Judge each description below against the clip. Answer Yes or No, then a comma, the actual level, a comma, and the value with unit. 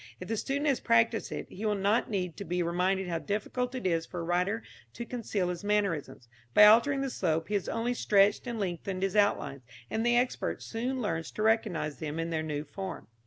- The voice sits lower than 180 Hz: No, high, 200 Hz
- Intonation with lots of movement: No, average, 4.6 semitones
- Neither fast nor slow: No, fast, 215 wpm